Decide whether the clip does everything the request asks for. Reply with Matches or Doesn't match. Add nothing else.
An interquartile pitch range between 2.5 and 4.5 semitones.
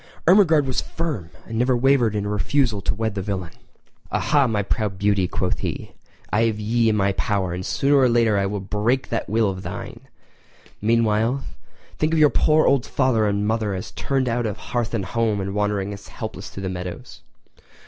Matches